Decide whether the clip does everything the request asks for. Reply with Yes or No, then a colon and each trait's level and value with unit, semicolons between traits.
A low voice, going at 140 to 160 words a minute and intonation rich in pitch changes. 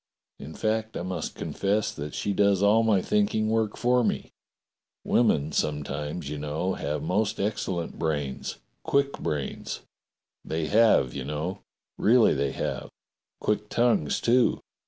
Yes: very low, 95 Hz; average, 145 wpm; wide, 6.7 semitones